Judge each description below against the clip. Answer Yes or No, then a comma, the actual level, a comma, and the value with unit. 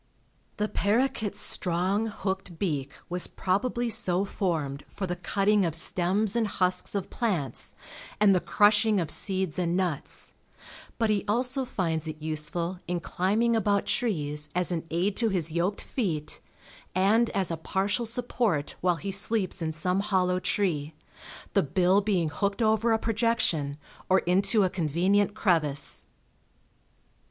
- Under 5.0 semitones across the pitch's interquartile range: Yes, average, 3.7 semitones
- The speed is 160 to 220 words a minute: No, average, 145 wpm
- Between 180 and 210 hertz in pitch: Yes, high, 190 Hz